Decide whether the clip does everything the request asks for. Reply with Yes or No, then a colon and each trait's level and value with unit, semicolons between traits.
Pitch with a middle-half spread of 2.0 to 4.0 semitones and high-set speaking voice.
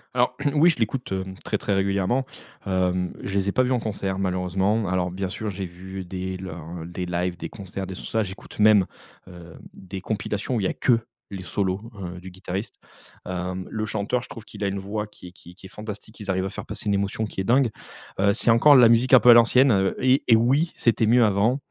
No: average, 3.5 semitones; low, 100 Hz